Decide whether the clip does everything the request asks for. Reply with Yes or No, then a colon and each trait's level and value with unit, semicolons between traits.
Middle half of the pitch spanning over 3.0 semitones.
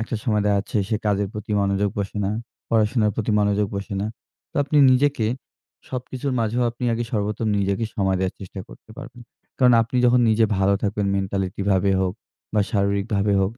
No: narrow, 2.6 semitones